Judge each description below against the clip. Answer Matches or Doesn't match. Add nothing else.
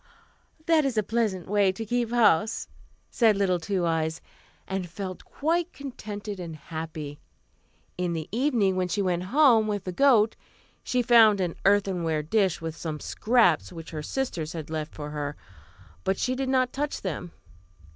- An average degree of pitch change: Doesn't match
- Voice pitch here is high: Matches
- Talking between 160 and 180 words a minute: Matches